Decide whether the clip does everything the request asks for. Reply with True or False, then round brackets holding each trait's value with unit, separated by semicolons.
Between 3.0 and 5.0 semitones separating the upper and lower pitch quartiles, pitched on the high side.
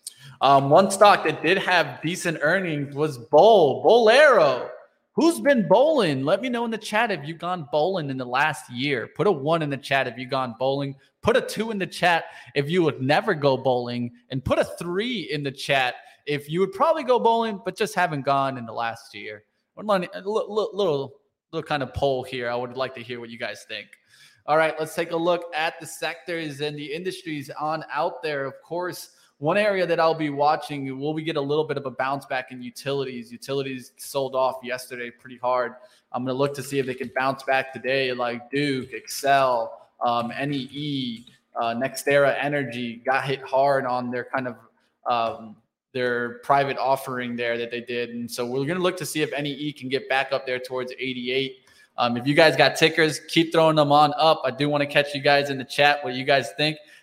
False (3.7 semitones; 140 Hz)